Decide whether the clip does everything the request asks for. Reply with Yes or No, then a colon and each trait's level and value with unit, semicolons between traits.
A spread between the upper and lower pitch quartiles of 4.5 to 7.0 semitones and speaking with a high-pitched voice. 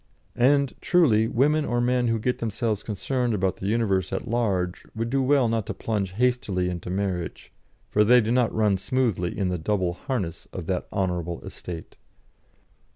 No: average, 4.8 semitones; low, 110 Hz